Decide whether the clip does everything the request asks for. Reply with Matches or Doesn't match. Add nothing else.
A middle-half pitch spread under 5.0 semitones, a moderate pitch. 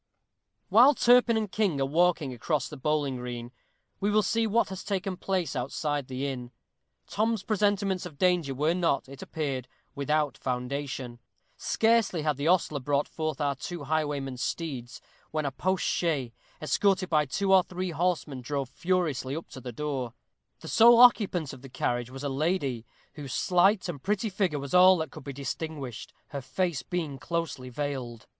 Doesn't match